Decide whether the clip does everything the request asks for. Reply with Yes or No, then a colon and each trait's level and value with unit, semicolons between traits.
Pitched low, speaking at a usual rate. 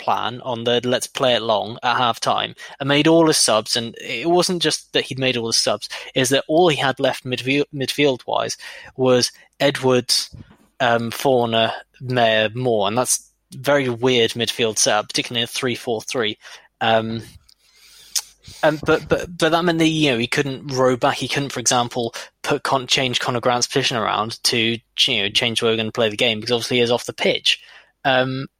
Yes: low, 125 Hz; average, 190 wpm